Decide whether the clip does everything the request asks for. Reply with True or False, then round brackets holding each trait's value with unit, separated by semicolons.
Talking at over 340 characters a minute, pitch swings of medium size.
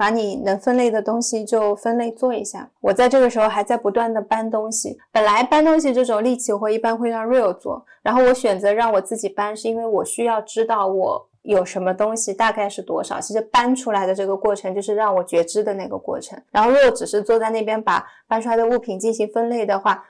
False (365 characters per minute; 2.3 semitones)